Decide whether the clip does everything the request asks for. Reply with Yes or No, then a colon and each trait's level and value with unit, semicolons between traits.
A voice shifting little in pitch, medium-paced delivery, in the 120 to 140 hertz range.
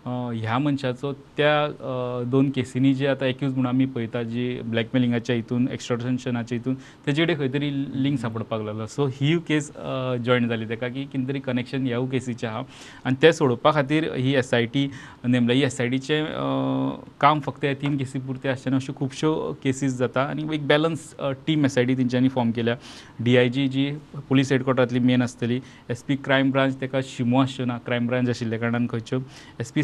Yes: narrow, 2.2 semitones; average, 180 wpm; low, 130 Hz